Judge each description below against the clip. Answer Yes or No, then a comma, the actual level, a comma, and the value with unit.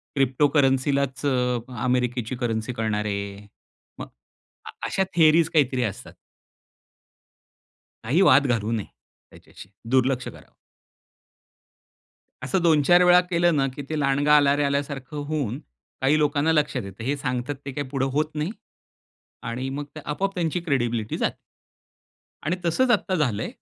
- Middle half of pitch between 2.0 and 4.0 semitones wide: Yes, average, 3.4 semitones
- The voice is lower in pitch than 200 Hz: Yes, medium, 140 Hz